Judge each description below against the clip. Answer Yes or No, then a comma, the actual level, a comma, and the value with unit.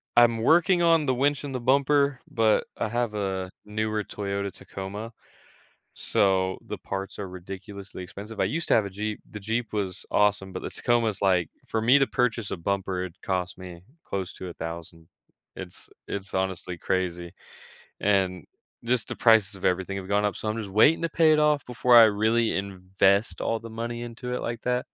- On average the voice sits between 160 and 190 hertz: No, low, 105 Hz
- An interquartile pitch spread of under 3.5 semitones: No, average, 3.8 semitones